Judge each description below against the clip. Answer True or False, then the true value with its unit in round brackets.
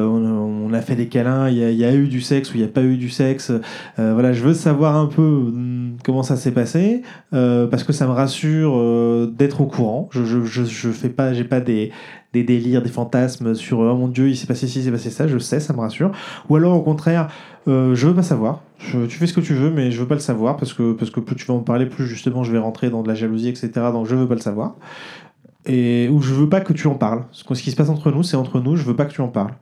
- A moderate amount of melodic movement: True (3.5 semitones)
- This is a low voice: True (130 Hz)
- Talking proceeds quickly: True (300 wpm)